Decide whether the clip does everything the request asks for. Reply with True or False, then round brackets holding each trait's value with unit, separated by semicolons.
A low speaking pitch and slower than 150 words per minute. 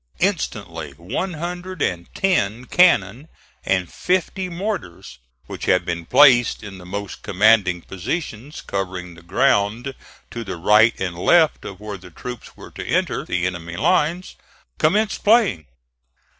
True (105 Hz; 140 wpm)